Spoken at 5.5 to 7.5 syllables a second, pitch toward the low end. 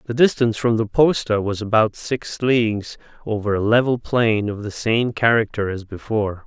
No: 5.0 syllables/s; low, 110 Hz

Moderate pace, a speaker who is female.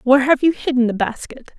No: fast, 225 wpm; female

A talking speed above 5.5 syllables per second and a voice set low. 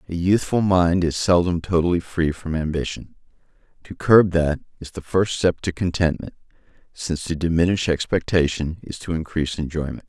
No: 5.3 syllables/s; very low, 85 Hz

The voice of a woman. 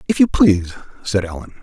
No: male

